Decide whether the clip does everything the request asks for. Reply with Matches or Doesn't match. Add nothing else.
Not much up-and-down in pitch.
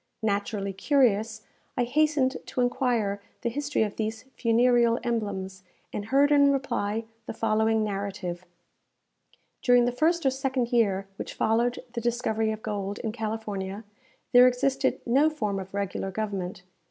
Doesn't match